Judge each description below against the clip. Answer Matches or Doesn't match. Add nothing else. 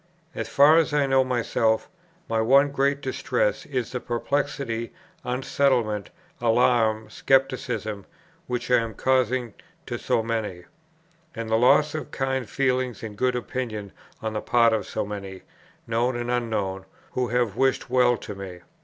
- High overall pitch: Doesn't match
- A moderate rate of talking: Matches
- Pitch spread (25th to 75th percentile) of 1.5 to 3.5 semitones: Matches